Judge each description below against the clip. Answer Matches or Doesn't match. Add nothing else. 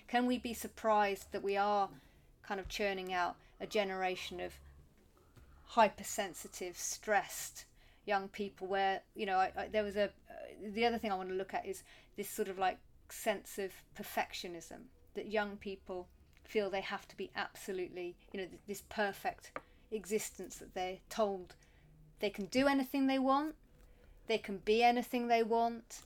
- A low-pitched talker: Doesn't match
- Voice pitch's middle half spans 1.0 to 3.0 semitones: Matches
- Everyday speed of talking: Matches